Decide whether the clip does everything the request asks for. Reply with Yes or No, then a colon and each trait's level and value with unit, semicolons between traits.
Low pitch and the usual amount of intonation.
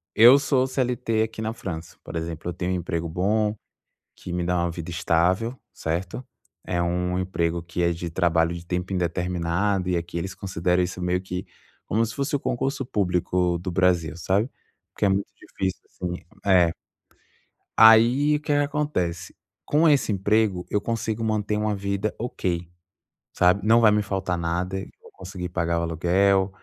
Yes: very low, 95 Hz; average, 3.9 semitones